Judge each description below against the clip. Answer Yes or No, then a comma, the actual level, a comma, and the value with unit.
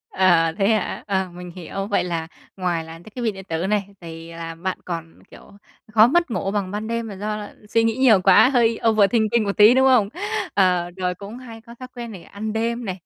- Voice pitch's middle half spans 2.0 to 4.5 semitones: Yes, average, 4.0 semitones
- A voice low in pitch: No, high, 200 Hz